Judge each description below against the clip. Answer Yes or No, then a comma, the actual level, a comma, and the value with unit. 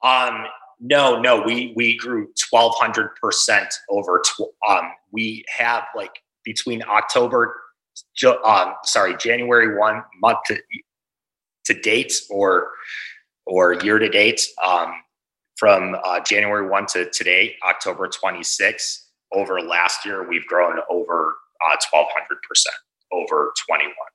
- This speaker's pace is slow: Yes, slow, 120 wpm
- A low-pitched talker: Yes, low, 125 Hz